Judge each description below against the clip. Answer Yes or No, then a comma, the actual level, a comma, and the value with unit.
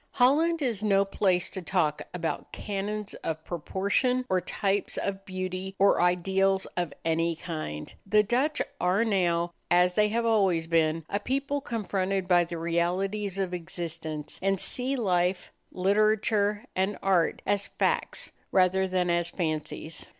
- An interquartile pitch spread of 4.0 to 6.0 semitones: No, average, 3.0 semitones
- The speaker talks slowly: No, average, 145 wpm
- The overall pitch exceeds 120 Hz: Yes, high, 190 Hz